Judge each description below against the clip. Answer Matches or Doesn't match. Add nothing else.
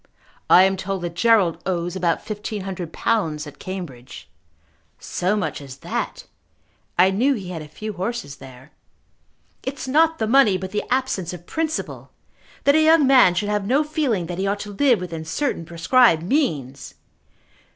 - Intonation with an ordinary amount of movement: Doesn't match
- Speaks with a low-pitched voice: Doesn't match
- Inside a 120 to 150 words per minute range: Doesn't match